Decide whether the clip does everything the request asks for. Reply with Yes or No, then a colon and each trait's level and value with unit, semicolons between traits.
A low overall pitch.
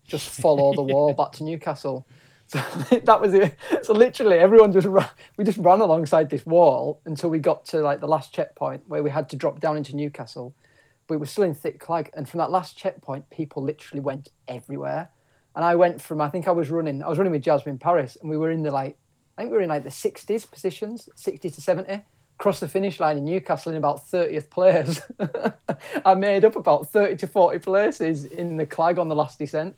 No: medium, 160 Hz